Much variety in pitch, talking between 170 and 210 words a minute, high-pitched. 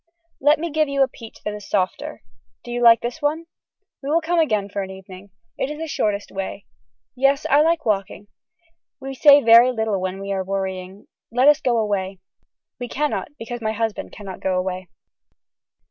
Yes: wide, 6.1 semitones; average, 190 wpm; high, 225 Hz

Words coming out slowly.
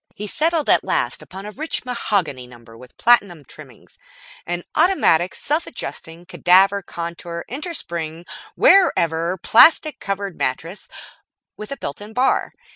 Yes: slow, 130 wpm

